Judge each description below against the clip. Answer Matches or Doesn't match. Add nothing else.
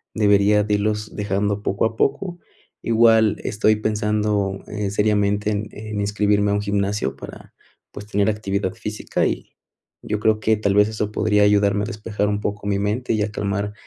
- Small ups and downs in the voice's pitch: Matches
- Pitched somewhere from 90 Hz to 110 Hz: Matches